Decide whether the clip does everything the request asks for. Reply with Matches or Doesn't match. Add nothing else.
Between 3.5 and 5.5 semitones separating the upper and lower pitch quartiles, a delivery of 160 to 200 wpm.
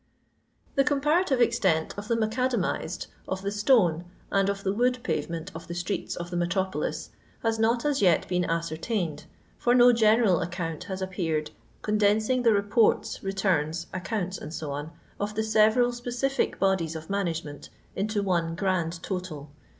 Doesn't match